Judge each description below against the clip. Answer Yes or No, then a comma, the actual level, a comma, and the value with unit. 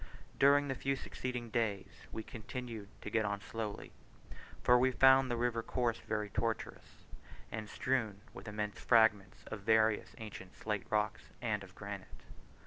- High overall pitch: No, low, 110 Hz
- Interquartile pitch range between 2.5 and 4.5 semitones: Yes, average, 2.8 semitones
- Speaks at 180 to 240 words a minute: No, average, 150 wpm